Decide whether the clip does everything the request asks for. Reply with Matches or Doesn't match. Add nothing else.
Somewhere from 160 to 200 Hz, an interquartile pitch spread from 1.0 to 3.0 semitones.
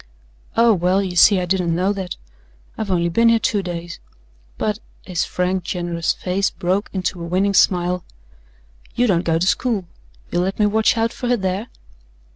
Matches